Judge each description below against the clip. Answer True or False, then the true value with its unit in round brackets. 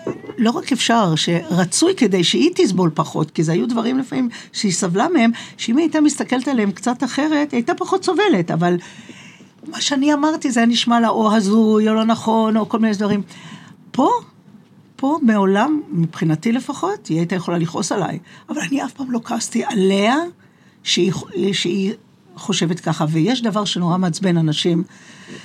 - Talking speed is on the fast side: True (165 wpm)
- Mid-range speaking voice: False (215 Hz)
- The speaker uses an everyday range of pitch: False (5.8 semitones)